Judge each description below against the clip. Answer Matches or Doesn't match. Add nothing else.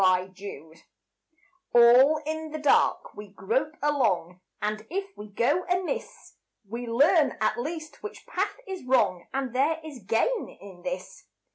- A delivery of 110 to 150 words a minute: Matches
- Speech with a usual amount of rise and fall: Doesn't match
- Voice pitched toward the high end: Matches